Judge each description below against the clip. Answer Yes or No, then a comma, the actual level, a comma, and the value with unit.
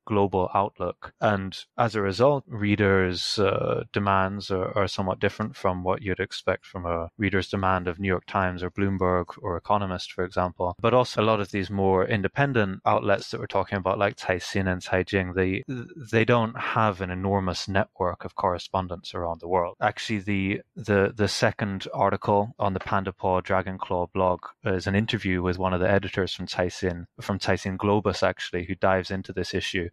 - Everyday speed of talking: Yes, average, 185 wpm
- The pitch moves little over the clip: Yes, narrow, 1.8 semitones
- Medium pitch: No, very low, 95 Hz